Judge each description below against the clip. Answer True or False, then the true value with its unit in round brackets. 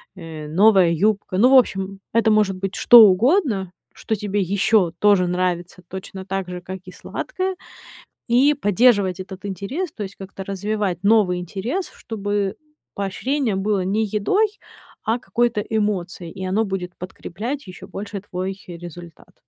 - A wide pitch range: False (3.0 semitones)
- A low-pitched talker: False (195 Hz)